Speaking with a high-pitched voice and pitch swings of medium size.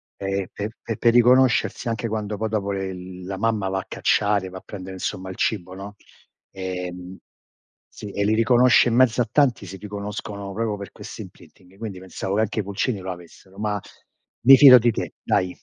No: low, 100 Hz; average, 3.0 semitones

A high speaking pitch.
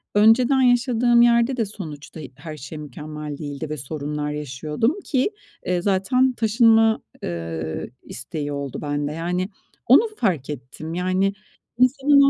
No: medium, 180 Hz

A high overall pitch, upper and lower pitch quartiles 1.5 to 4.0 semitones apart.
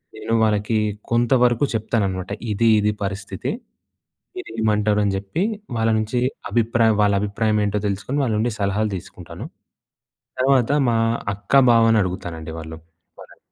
No: low, 110 Hz; average, 2.7 semitones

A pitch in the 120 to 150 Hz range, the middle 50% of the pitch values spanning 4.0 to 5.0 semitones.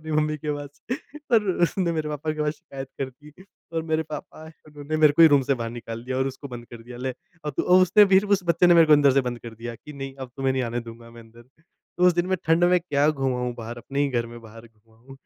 Yes: medium, 140 Hz; average, 4.7 semitones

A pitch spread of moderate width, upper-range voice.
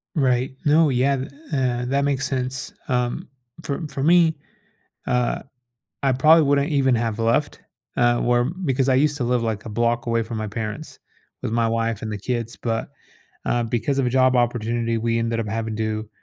No: average, 3.0 semitones; low, 125 Hz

